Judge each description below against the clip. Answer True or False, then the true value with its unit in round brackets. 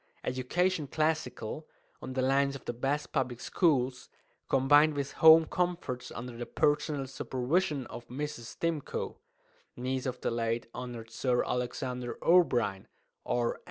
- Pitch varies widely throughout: False (3.5 semitones)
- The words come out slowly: True (130 wpm)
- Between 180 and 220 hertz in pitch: False (130 Hz)